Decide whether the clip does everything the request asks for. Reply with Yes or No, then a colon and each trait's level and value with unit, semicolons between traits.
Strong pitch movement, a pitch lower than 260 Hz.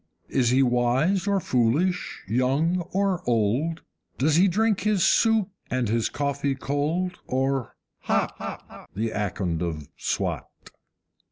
Yes: wide, 7.1 semitones; medium, 140 Hz